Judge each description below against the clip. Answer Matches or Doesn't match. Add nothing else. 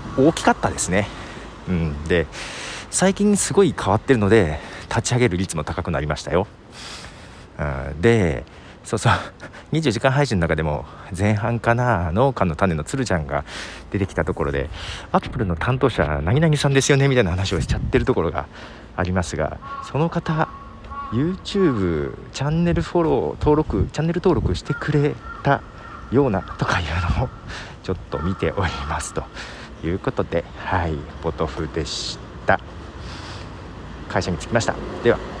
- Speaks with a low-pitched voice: Matches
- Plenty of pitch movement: Matches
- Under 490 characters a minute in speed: Matches